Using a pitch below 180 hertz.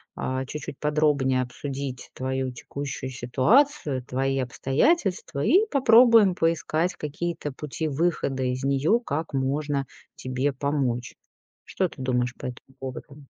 Yes: medium, 140 Hz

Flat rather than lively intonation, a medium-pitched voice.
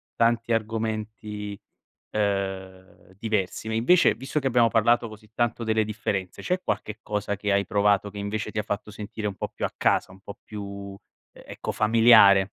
No: narrow, 1.9 semitones; low, 105 Hz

